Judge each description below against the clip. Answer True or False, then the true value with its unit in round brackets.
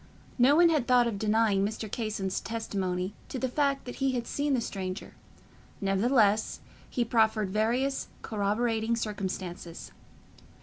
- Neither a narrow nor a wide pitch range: True (3.7 semitones)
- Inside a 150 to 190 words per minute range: False (135 wpm)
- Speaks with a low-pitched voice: False (220 Hz)